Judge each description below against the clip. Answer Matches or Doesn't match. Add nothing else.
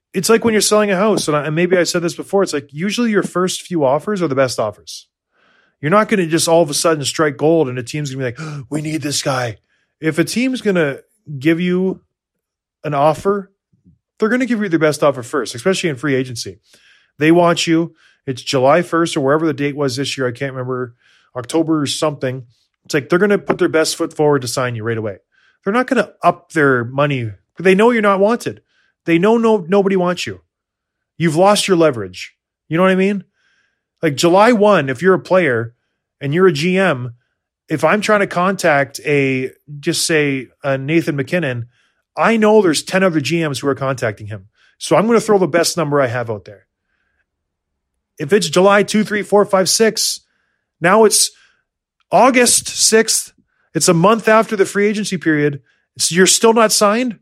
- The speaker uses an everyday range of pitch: Doesn't match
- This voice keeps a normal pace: Doesn't match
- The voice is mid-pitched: Matches